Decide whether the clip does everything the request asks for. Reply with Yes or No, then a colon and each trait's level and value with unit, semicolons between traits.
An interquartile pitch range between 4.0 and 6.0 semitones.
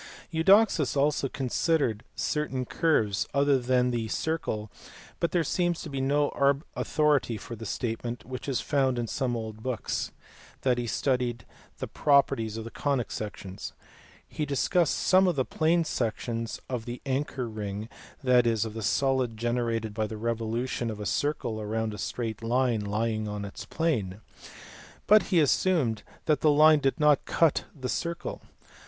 Yes: average, 4.6 semitones